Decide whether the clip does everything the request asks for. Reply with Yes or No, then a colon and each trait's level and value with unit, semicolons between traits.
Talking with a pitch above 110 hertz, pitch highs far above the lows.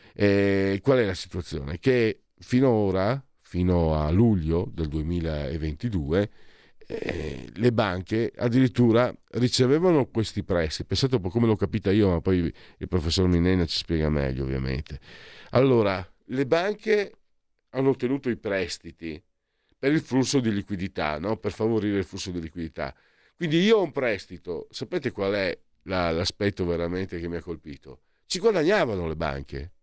No: very low, 95 Hz; wide, 6.2 semitones